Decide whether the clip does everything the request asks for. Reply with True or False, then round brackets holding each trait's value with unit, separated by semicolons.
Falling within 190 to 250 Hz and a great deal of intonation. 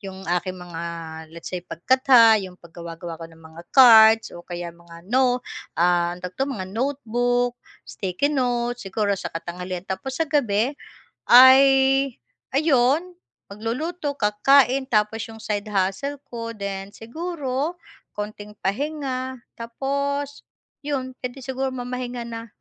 True (230 Hz; 5.8 semitones)